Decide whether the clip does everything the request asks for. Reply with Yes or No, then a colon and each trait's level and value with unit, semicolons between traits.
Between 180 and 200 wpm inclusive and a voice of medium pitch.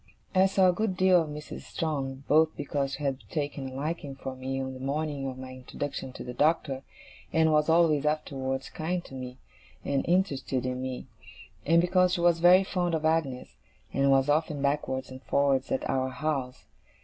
Yes: average, 190 wpm; medium, 145 Hz